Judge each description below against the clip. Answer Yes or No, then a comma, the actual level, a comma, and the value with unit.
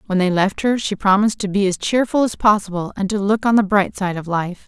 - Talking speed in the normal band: No, fast, 270 wpm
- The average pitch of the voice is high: Yes, high, 200 Hz